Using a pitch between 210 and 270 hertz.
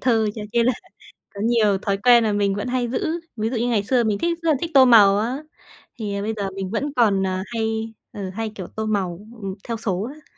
Yes: high, 220 Hz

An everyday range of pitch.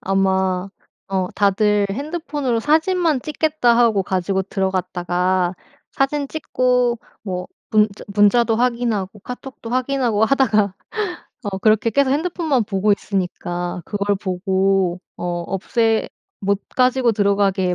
Yes: average, 4.8 semitones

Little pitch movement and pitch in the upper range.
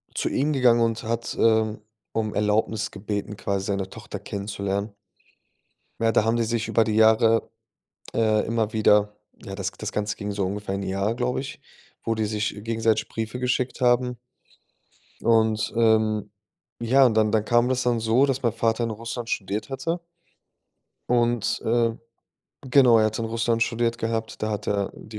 No: narrow, 1.9 semitones; low, 110 Hz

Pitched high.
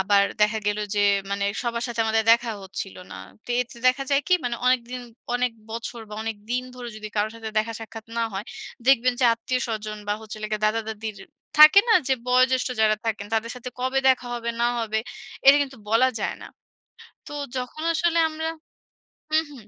Yes: high, 230 Hz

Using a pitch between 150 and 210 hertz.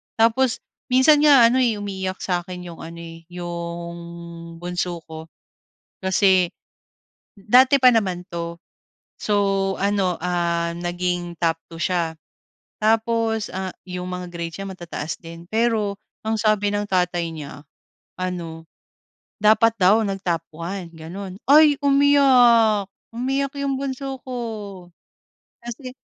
Yes: high, 190 Hz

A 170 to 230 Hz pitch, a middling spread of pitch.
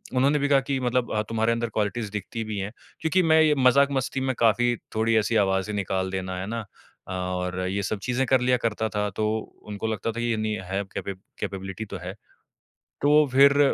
No: low, 110 Hz; average, 4.4 semitones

